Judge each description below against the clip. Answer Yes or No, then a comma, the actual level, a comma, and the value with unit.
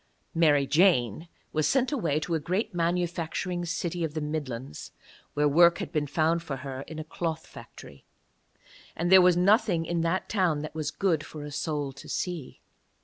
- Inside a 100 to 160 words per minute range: No, average, 180 wpm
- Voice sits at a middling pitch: Yes, medium, 165 Hz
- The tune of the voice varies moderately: Yes, average, 3.0 semitones